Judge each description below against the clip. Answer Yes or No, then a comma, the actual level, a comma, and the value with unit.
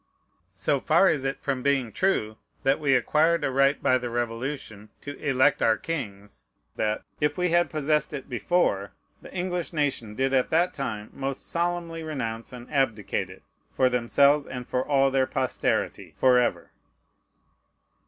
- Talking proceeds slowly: No, average, 155 wpm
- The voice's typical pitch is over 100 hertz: Yes, low, 135 Hz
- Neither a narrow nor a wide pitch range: Yes, average, 3.9 semitones